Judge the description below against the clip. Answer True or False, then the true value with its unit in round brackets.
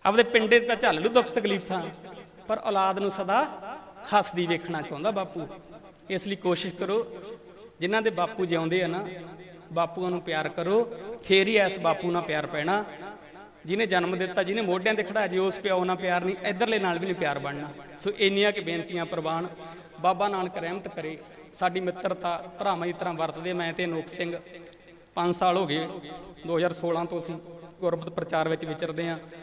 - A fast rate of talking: True (175 wpm)